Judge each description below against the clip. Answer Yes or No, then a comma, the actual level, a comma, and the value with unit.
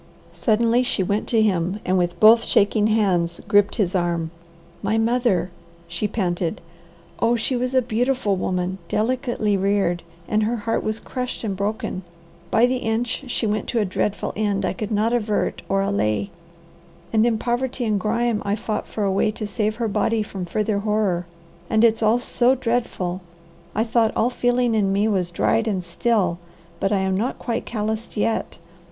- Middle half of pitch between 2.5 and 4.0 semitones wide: Yes, average, 2.9 semitones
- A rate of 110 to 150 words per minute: No, average, 180 wpm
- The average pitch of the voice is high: Yes, high, 215 Hz